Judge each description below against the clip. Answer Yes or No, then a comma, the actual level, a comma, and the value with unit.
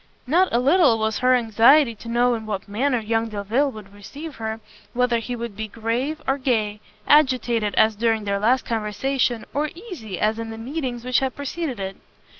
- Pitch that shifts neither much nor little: Yes, average, 3.5 semitones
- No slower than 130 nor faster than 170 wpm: No, average, 190 wpm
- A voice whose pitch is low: No, high, 235 Hz